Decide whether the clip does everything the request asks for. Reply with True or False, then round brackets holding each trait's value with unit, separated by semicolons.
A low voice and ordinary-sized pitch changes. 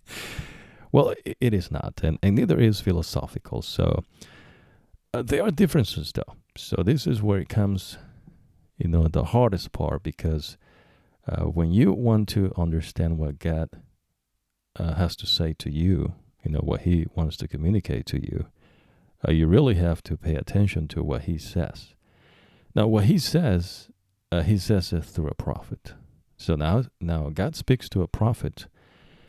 True (90 Hz; 4.5 semitones)